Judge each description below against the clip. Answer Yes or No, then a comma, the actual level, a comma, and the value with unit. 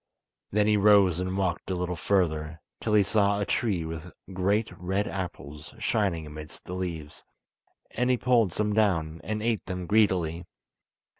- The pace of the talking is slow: No, average, 160 wpm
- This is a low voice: Yes, very low, 95 Hz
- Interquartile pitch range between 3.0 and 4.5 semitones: Yes, average, 4.0 semitones